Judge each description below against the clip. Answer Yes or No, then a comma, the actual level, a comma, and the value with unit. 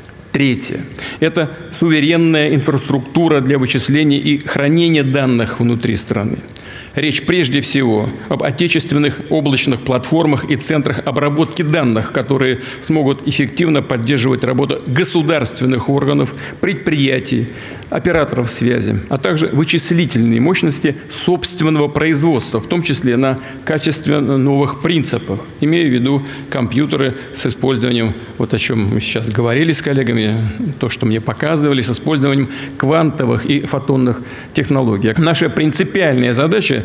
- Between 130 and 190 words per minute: No, average, 115 wpm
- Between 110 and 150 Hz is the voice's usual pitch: Yes, medium, 140 Hz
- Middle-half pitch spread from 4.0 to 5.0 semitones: No, average, 3.4 semitones